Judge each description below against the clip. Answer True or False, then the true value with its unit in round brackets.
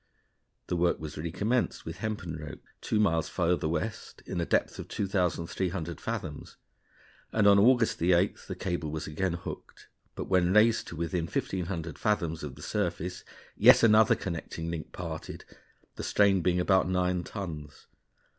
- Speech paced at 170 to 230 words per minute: False (155 wpm)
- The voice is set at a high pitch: False (90 Hz)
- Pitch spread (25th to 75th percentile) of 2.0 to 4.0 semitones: True (3.0 semitones)